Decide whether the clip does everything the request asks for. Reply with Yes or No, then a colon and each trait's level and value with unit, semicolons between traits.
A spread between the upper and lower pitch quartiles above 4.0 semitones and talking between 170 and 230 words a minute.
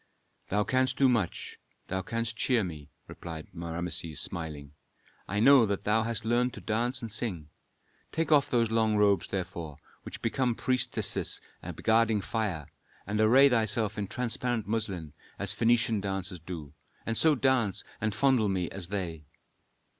No: average, 4.4 semitones; average, 150 wpm